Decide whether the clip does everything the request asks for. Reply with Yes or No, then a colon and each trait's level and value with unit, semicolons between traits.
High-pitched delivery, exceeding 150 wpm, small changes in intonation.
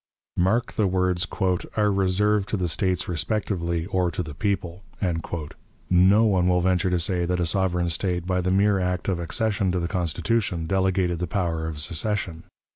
No: very low, 90 Hz; average, 175 wpm; narrow, 2.1 semitones